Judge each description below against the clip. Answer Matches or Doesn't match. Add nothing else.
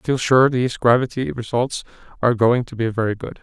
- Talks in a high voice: Doesn't match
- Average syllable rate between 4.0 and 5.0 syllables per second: Doesn't match